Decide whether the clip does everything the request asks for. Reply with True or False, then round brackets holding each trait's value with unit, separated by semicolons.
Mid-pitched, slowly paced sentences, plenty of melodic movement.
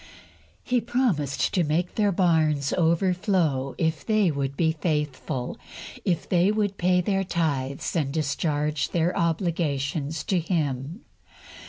False (165 Hz; 125 wpm; 3.8 semitones)